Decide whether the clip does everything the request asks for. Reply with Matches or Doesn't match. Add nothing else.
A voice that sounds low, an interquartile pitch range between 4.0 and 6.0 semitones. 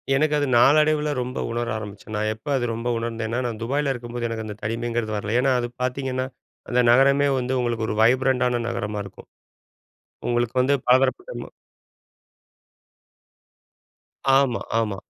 Doesn't match